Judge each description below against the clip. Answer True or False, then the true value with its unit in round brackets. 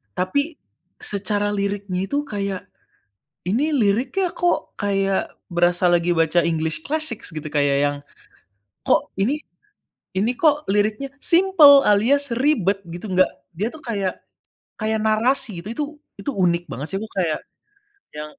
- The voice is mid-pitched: False (205 Hz)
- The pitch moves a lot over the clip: True (7.3 semitones)